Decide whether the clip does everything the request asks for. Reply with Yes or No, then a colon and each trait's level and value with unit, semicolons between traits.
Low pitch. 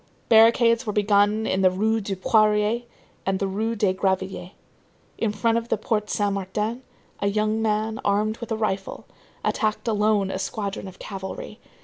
No: high, 210 Hz